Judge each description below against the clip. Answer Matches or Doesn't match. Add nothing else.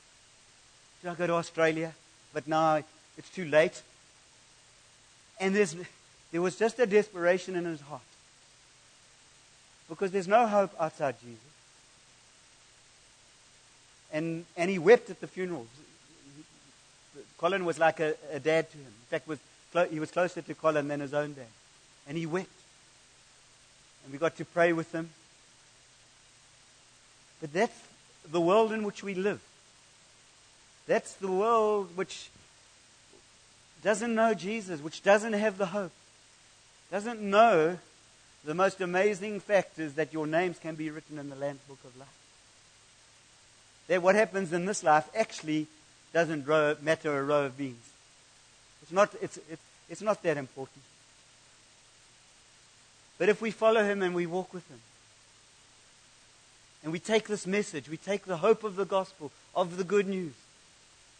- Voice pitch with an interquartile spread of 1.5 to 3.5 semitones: Doesn't match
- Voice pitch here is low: Doesn't match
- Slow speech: Doesn't match